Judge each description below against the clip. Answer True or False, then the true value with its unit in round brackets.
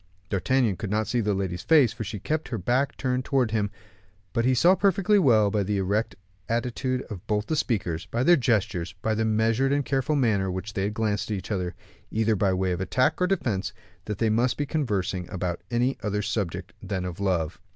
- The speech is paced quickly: True (215 wpm)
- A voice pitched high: False (110 Hz)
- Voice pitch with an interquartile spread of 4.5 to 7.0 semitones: True (4.8 semitones)